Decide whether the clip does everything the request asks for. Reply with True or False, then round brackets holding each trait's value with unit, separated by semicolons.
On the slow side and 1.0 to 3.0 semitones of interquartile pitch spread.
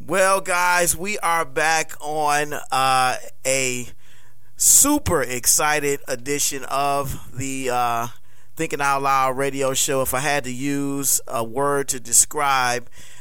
True (125 wpm; 2.7 semitones)